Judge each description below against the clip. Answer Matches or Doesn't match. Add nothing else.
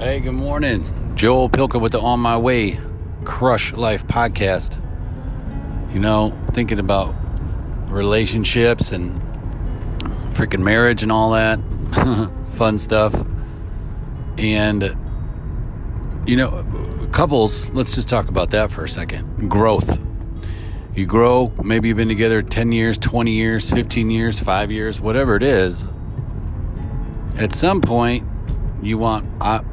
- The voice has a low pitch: Matches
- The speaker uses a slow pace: Matches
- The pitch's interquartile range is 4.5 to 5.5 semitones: Doesn't match